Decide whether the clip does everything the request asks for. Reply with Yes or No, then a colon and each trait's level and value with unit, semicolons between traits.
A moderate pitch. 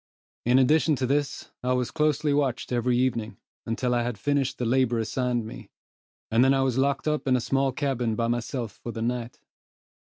No: low, 125 Hz